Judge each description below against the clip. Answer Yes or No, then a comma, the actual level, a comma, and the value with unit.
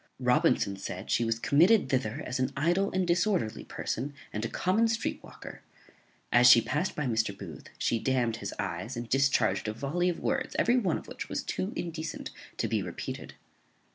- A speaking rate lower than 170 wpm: No, average, 185 wpm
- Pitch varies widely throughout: Yes, wide, 7.9 semitones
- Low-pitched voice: Yes, low, 130 Hz